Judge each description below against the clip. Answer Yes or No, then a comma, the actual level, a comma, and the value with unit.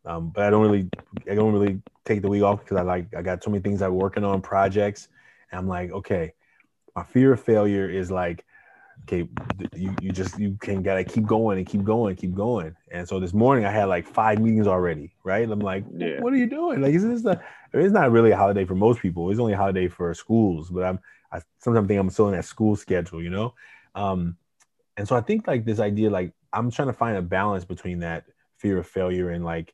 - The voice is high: No, low, 100 Hz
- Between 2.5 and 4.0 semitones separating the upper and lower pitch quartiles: Yes, average, 3.1 semitones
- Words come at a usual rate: No, fast, 245 wpm